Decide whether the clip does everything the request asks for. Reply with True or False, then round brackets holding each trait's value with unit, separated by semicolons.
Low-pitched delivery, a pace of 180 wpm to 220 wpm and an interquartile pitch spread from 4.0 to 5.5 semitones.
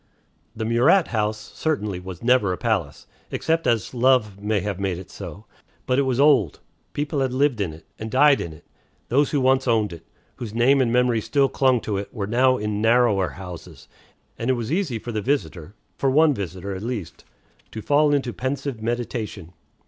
True (115 Hz; 195 wpm; 4.8 semitones)